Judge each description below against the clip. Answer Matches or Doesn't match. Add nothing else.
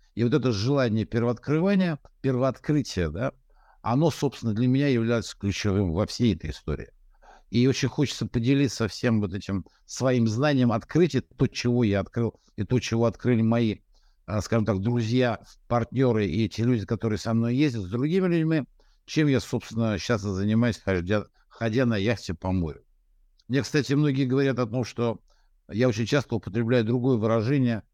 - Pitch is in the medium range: Doesn't match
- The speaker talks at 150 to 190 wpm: Matches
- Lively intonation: Doesn't match